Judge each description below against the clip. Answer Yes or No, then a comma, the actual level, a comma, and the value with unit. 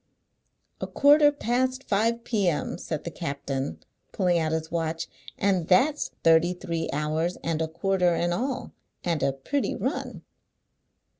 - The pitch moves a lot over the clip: Yes, wide, 6.2 semitones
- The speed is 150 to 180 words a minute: No, average, 140 wpm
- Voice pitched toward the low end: No, medium, 175 Hz